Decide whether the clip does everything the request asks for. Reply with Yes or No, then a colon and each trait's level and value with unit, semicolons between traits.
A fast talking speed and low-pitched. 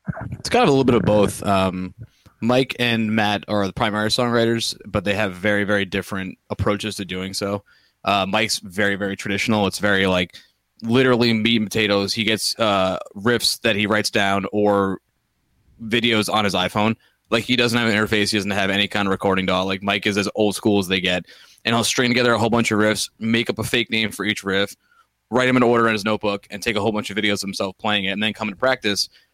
Yes: fast, 235 wpm; low, 105 Hz